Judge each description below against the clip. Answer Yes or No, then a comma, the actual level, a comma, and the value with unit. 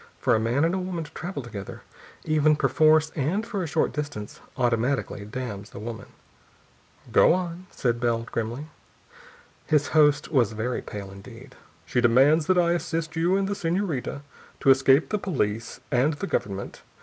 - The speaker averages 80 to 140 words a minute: No, average, 160 wpm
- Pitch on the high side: No, medium, 145 Hz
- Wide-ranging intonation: Yes, wide, 5.8 semitones